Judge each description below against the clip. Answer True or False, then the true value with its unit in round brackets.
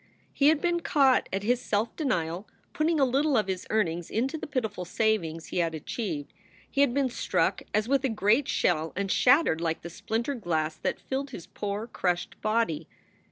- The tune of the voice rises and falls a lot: True (7.5 semitones)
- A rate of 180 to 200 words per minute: True (190 wpm)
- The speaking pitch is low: False (220 Hz)